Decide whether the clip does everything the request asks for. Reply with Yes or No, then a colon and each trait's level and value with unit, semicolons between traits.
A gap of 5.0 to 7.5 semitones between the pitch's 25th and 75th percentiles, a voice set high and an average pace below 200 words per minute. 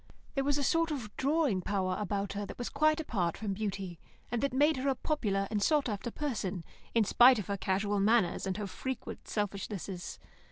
No: wide, 5.6 semitones; high, 210 Hz; fast, 205 wpm